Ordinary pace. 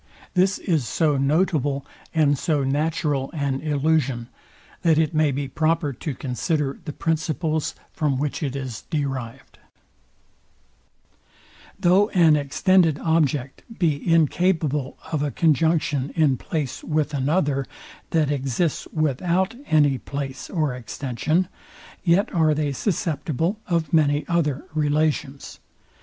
No: slow, 120 wpm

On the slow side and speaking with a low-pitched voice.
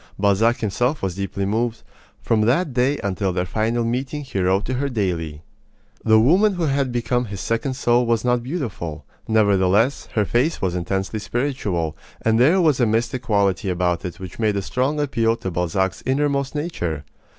No: average, 175 wpm; low, 115 Hz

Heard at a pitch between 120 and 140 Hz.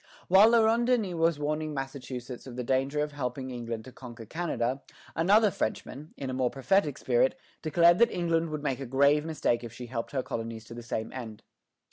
Yes: low, 135 Hz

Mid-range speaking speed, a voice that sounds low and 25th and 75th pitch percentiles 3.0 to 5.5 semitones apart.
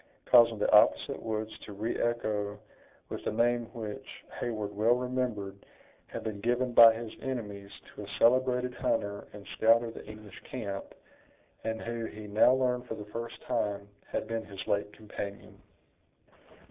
No: average, 160 wpm; low, 110 Hz; narrow, 2.6 semitones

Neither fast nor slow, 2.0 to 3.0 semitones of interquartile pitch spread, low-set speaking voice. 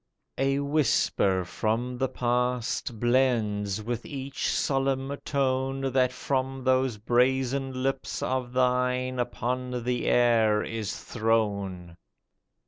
No: slow, 105 wpm; narrow, 2.6 semitones; low, 125 Hz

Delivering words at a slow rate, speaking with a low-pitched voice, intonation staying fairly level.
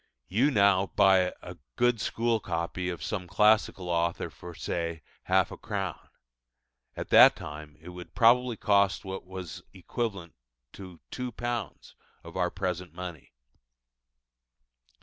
No: slow, 130 wpm; very low, 95 Hz; average, 3.5 semitones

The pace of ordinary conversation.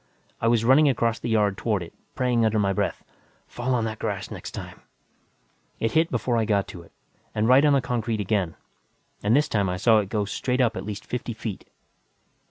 No: fast, 210 wpm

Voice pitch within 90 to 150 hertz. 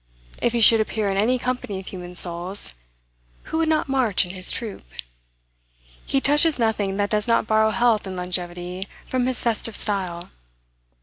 No: high, 210 Hz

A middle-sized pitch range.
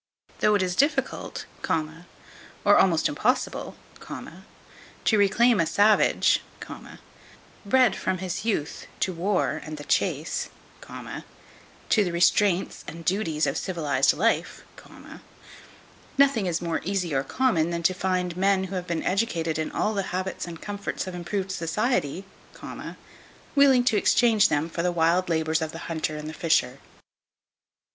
Yes: average, 3.9 semitones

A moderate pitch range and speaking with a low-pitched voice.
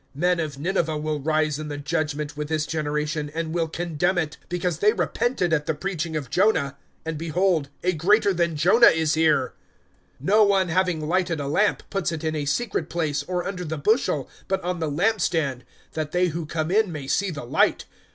No: average, 3.1 semitones; medium, 160 Hz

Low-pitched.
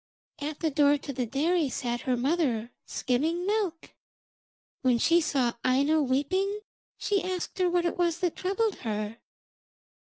No: very high, 305 Hz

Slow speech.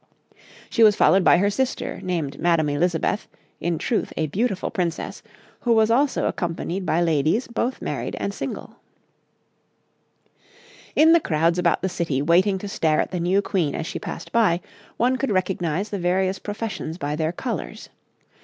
No: average, 165 wpm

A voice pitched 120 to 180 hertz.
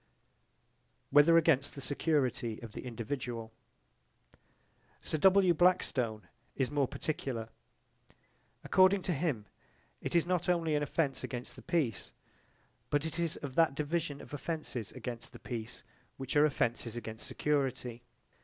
Yes: medium, 140 Hz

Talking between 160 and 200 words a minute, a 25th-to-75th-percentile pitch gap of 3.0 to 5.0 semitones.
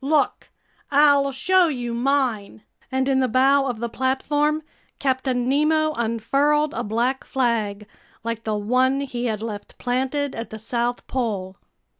No: average, 145 wpm; average, 3.4 semitones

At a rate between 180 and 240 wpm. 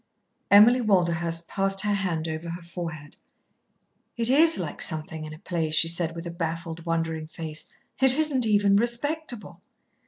No: average, 155 wpm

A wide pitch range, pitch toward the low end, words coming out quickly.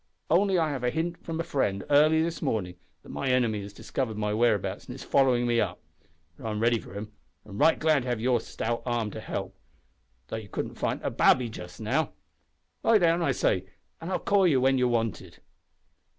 Yes: wide, 6.5 semitones; low, 125 Hz; fast, 215 wpm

